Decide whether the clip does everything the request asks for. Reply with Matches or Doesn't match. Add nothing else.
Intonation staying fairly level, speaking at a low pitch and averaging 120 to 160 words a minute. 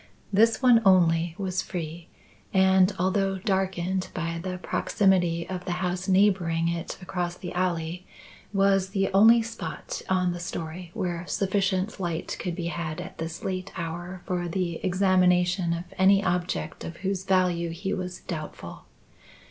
Doesn't match